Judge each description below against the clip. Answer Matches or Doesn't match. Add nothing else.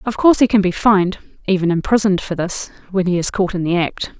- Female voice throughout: Matches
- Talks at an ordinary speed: Doesn't match